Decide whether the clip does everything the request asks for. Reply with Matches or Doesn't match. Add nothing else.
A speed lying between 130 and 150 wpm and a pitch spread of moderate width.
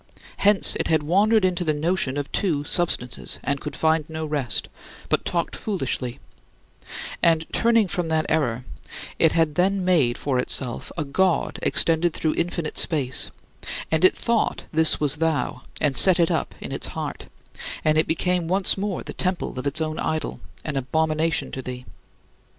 Doesn't match